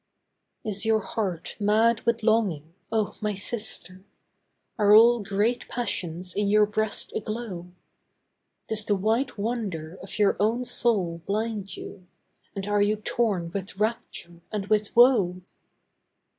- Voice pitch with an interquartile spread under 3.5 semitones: Yes, average, 2.8 semitones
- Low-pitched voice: No, high, 210 Hz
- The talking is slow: Yes, slow, 130 wpm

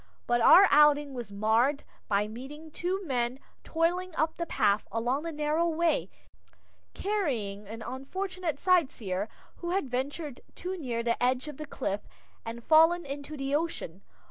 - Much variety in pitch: Yes, wide, 5.8 semitones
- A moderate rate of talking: Yes, average, 150 wpm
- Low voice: No, very high, 285 Hz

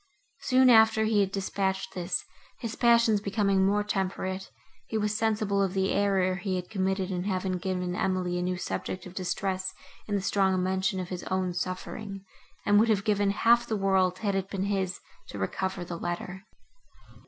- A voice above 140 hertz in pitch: Yes, high, 190 Hz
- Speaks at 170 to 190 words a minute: Yes, average, 180 wpm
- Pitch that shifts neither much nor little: No, narrow, 1.8 semitones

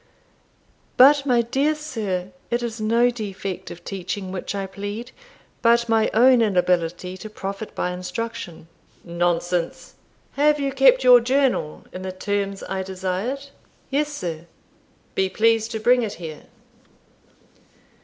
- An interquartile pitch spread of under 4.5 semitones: No, average, 4.8 semitones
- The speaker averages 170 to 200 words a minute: No, slow, 135 wpm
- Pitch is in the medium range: No, high, 215 Hz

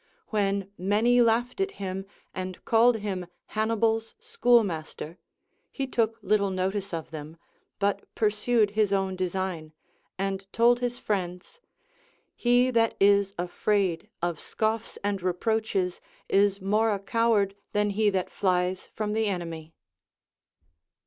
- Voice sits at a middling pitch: No, high, 200 Hz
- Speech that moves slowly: Yes, slow, 125 wpm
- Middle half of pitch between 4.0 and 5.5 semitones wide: No, average, 3.2 semitones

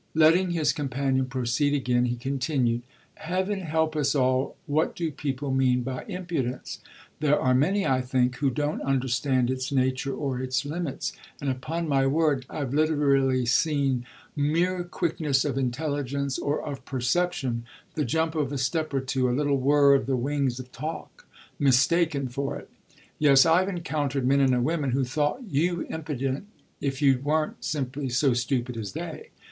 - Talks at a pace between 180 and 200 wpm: No, average, 165 wpm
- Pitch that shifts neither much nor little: Yes, average, 3.1 semitones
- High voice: No, medium, 140 Hz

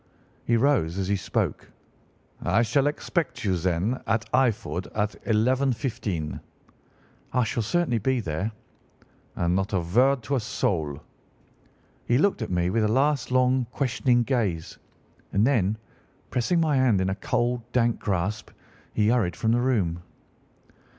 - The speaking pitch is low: Yes, low, 115 Hz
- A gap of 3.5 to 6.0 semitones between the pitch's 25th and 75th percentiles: Yes, average, 5.1 semitones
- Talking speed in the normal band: Yes, average, 145 wpm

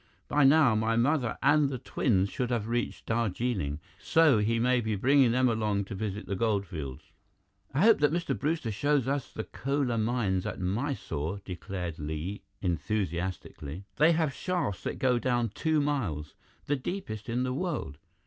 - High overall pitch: No, low, 115 Hz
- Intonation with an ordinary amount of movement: No, wide, 5.9 semitones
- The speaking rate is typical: Yes, average, 170 wpm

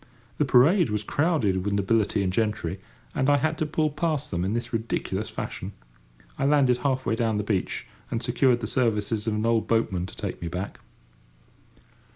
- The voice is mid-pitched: No, low, 115 Hz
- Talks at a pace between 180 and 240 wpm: Yes, average, 190 wpm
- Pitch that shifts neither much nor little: Yes, average, 4.9 semitones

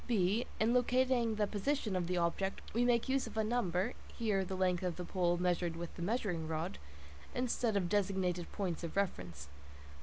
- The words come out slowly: No, average, 185 wpm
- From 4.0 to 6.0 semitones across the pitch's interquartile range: Yes, average, 4.7 semitones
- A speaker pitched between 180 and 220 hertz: Yes, high, 190 Hz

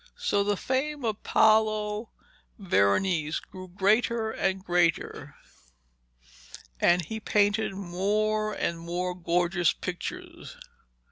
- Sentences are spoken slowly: Yes, slow, 95 wpm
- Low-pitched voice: No, high, 195 Hz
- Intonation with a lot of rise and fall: No, average, 3.4 semitones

